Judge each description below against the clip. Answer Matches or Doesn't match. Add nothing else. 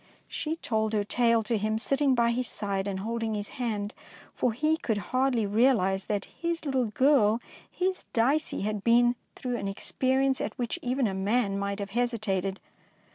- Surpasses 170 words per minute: Matches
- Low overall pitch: Doesn't match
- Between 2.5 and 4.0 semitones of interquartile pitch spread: Matches